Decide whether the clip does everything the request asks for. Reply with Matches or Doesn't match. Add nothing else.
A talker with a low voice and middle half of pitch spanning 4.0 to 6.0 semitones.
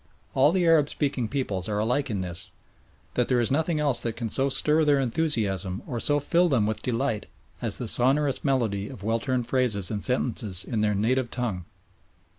Matches